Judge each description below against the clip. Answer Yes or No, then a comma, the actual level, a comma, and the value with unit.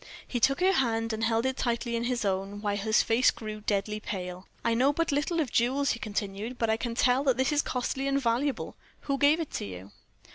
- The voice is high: Yes, high, 235 Hz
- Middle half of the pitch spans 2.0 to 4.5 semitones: Yes, average, 4.1 semitones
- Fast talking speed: Yes, fast, 230 wpm